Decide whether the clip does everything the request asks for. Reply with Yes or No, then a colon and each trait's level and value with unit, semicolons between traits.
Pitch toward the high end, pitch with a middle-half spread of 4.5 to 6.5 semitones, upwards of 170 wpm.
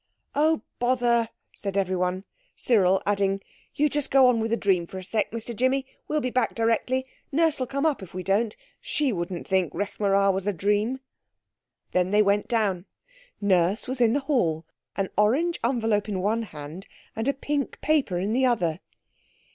Yes: high, 215 Hz; average, 5.0 semitones; average, 180 wpm